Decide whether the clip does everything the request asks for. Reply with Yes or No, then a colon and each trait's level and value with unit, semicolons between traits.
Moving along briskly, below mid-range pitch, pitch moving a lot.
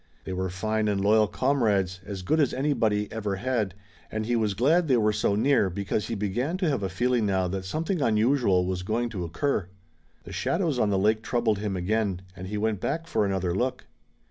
No: fast, 210 wpm; low, 105 Hz; average, 4.3 semitones